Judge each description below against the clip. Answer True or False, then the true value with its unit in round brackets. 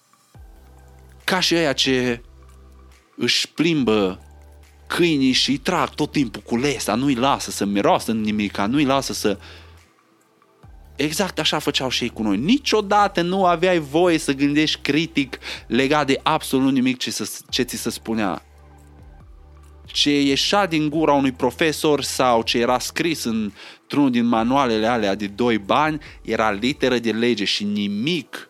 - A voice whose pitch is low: True (125 Hz)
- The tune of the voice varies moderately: False (7.7 semitones)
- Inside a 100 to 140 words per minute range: False (150 wpm)